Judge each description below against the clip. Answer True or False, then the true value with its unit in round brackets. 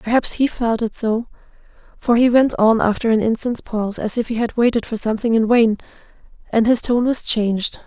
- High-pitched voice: True (230 Hz)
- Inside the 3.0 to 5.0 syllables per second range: False (5.5 syllables/s)